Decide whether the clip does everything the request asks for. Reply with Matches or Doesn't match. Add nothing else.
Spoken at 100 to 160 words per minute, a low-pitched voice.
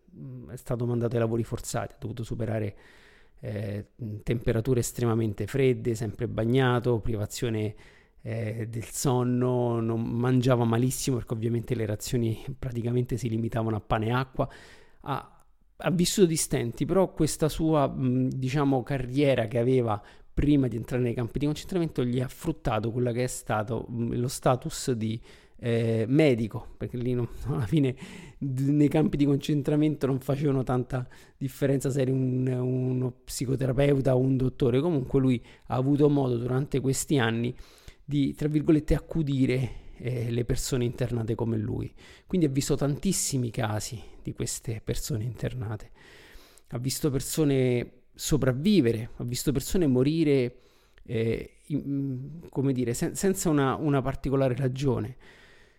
Matches